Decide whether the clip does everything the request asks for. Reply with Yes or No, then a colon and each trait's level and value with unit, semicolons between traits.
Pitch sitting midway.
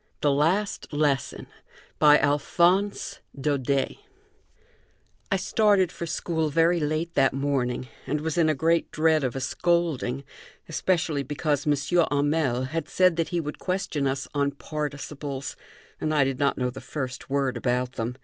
Yes: medium, 150 Hz